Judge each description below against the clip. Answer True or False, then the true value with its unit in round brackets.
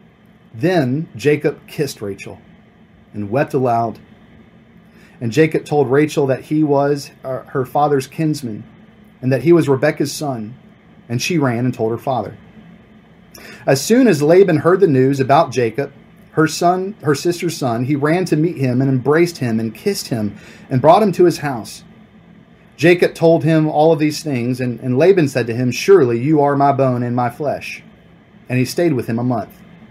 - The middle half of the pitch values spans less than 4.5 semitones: False (4.9 semitones)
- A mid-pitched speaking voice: True (145 Hz)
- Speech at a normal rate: True (180 wpm)